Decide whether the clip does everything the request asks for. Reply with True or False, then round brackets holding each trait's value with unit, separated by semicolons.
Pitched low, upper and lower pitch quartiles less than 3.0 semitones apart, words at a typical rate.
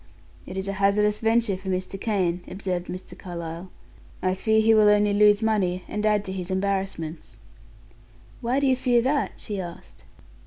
False (195 Hz; 2.6 semitones; 170 wpm)